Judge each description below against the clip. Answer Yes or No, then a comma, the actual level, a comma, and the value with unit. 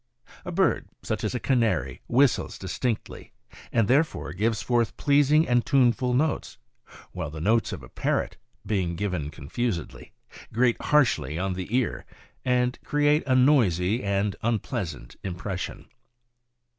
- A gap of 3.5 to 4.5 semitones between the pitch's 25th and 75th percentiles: No, wide, 5.5 semitones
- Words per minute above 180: No, slow, 135 wpm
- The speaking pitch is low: Yes, low, 115 Hz